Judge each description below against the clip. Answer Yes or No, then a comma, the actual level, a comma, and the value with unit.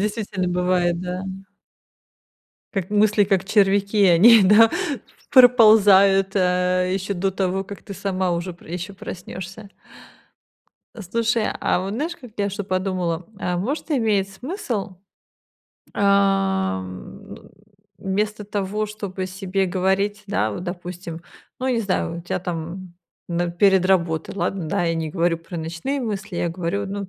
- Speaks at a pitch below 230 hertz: Yes, high, 190 Hz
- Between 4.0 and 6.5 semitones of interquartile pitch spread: No, narrow, 2.4 semitones